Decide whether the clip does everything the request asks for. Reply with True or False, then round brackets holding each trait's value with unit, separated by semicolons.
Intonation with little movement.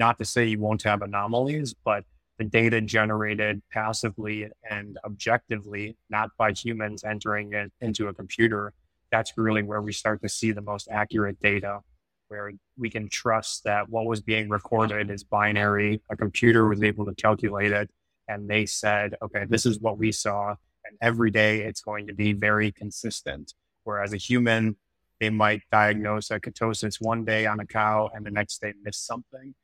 True (1.3 semitones)